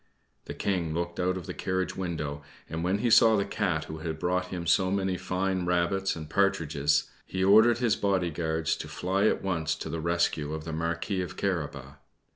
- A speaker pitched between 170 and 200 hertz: No, very low, 90 Hz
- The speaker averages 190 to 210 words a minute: Yes, average, 195 wpm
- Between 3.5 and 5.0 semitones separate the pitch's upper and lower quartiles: No, average, 3.1 semitones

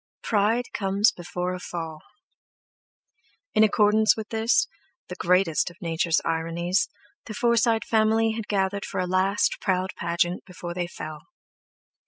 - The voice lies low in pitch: No, high, 190 Hz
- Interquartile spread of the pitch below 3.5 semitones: No, average, 3.9 semitones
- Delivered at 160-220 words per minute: No, slow, 135 wpm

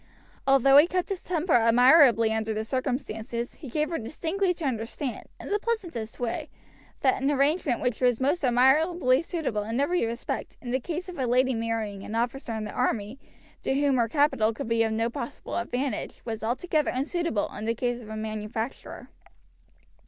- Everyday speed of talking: Yes, average, 180 wpm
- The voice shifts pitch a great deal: No, average, 4.6 semitones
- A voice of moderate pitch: No, very high, 250 Hz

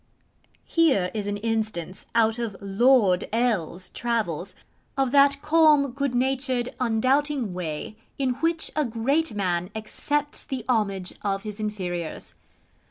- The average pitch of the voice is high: Yes, high, 230 Hz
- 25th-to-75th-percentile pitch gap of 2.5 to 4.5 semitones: No, wide, 5.5 semitones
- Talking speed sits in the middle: No, slow, 130 wpm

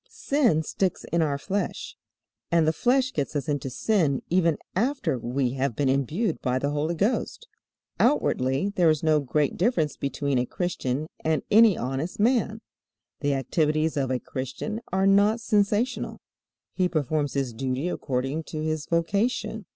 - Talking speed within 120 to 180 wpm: Yes, average, 155 wpm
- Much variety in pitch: Yes, wide, 6.5 semitones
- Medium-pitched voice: Yes, medium, 155 Hz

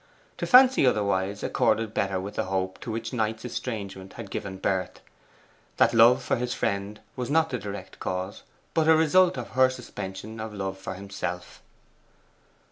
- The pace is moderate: Yes, average, 165 wpm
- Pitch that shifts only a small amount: No, average, 4.5 semitones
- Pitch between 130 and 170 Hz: No, low, 105 Hz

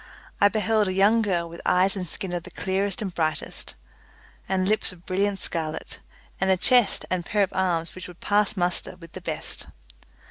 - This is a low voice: No, medium, 185 Hz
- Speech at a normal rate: Yes, average, 190 wpm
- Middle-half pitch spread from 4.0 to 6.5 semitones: No, narrow, 2.4 semitones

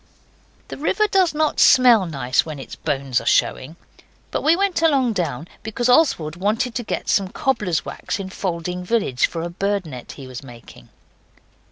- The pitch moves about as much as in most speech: No, wide, 8.6 semitones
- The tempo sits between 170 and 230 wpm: Yes, average, 175 wpm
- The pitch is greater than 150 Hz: Yes, high, 190 Hz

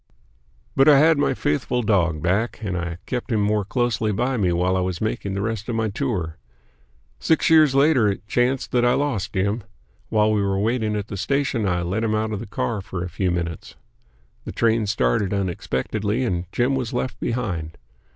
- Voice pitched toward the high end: No, low, 105 Hz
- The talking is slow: No, average, 200 wpm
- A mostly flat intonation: No, average, 4.7 semitones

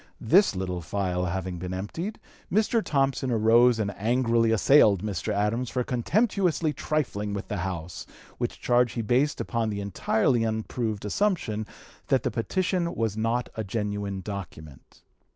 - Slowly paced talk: No, average, 145 wpm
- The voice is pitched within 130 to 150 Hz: No, low, 110 Hz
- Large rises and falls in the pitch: No, average, 4.3 semitones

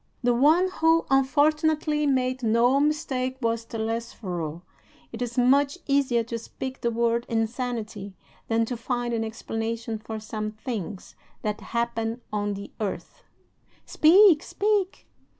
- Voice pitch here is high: Yes, high, 235 Hz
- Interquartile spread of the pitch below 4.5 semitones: Yes, average, 3.7 semitones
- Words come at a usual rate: No, slow, 130 wpm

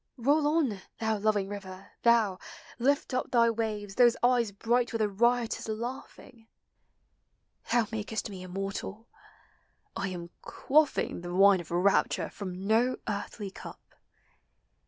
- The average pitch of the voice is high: Yes, high, 220 Hz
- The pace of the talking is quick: No, slow, 135 wpm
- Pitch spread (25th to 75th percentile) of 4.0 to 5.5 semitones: No, average, 3.4 semitones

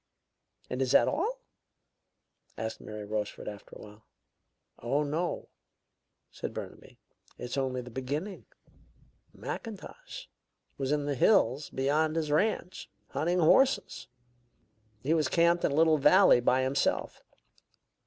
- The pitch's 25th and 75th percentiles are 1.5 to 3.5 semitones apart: No, average, 5.2 semitones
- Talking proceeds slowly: Yes, slow, 125 wpm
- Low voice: No, medium, 145 Hz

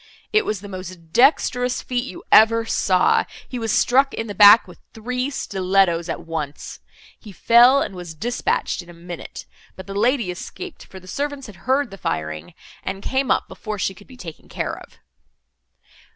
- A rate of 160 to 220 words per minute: Yes, average, 180 wpm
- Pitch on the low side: No, high, 205 Hz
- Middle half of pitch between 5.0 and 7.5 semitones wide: Yes, wide, 5.4 semitones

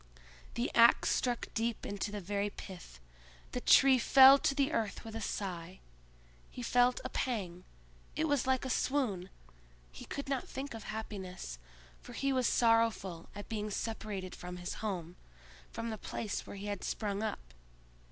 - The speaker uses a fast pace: No, average, 160 wpm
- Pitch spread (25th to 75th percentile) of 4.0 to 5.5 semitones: Yes, average, 4.6 semitones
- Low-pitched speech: No, high, 215 Hz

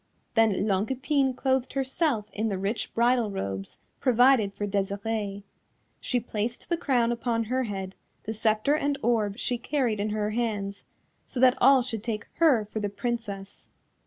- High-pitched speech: Yes, high, 225 Hz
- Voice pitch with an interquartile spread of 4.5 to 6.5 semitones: No, average, 3.7 semitones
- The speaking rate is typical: Yes, average, 160 wpm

